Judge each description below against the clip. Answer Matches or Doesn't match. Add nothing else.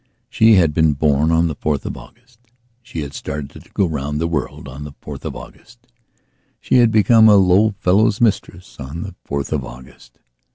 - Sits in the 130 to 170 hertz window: Doesn't match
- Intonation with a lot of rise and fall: Matches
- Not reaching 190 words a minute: Doesn't match